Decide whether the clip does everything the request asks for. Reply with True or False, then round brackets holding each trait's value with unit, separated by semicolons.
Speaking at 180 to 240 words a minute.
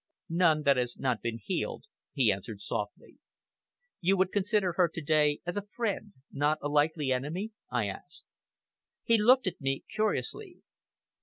False (155 wpm)